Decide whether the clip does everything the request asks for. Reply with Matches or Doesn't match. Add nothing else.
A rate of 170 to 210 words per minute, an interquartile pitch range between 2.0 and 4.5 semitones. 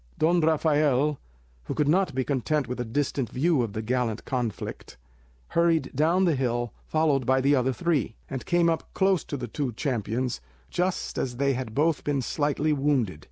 Matches